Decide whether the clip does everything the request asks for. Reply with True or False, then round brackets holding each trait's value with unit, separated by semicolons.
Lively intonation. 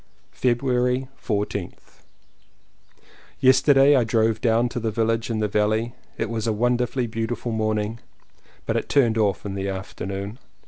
False (2.6 semitones)